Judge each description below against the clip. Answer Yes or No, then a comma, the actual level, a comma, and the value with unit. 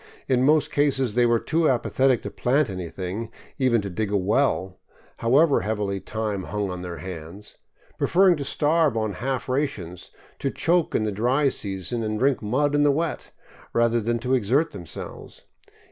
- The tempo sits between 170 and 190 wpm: Yes, average, 175 wpm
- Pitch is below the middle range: Yes, low, 120 Hz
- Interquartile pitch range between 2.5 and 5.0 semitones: No, wide, 5.4 semitones